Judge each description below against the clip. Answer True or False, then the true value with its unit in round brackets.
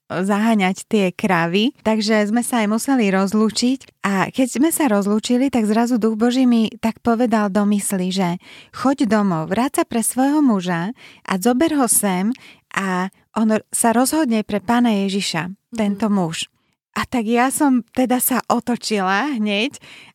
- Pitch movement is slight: False (3.6 semitones)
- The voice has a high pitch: True (220 Hz)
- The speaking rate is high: False (150 wpm)